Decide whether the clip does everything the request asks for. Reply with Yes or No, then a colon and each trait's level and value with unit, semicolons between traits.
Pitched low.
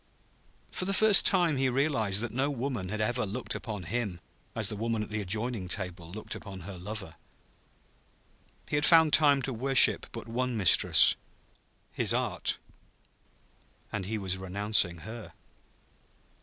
Yes: low, 110 Hz